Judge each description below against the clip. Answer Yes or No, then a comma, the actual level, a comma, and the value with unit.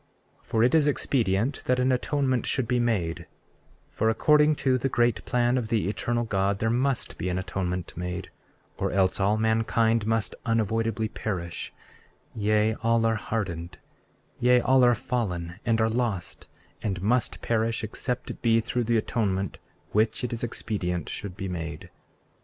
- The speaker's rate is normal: Yes, average, 165 wpm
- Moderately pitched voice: No, low, 110 Hz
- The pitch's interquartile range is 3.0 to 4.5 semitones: Yes, average, 3.8 semitones